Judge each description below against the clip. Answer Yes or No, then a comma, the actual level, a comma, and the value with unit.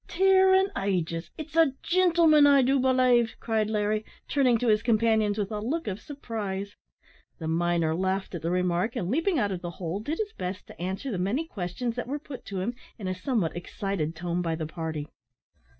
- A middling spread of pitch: No, wide, 6.8 semitones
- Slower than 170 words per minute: No, average, 200 wpm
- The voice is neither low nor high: No, high, 210 Hz